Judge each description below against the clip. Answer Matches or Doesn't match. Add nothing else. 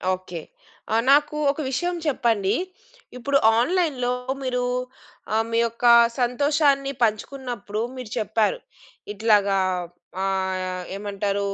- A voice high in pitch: Matches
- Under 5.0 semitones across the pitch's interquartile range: Doesn't match